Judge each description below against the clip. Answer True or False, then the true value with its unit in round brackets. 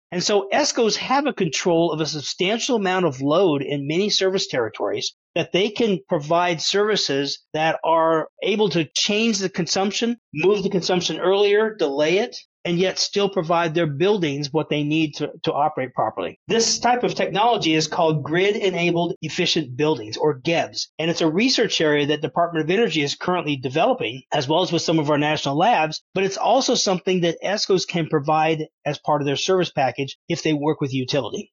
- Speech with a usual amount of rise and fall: True (4.1 semitones)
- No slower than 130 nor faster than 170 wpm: False (190 wpm)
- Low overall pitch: False (170 Hz)